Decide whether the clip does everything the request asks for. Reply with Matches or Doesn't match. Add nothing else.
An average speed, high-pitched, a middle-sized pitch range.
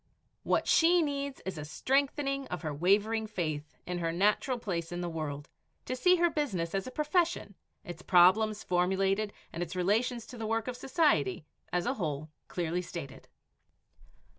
Doesn't match